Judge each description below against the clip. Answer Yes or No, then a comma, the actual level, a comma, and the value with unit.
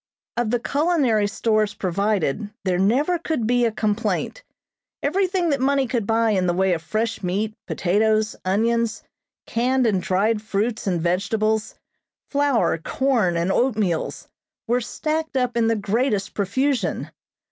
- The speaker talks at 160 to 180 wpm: No, average, 140 wpm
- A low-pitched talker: No, high, 220 Hz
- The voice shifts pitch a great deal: No, average, 4.1 semitones